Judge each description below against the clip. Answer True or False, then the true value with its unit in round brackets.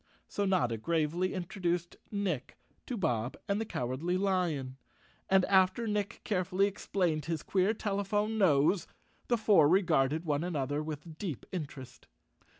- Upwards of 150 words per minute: False (135 wpm)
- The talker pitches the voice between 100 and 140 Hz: False (175 Hz)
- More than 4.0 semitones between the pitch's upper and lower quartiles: True (4.7 semitones)